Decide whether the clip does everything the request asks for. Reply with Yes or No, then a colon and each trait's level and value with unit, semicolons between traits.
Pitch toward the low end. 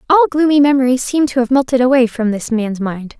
No: very high, 255 Hz